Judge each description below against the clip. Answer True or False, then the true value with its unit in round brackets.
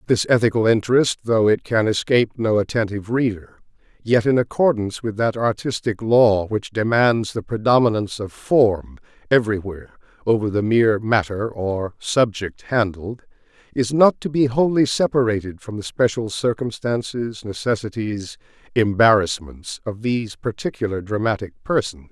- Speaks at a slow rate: True (130 wpm)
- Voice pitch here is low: True (110 Hz)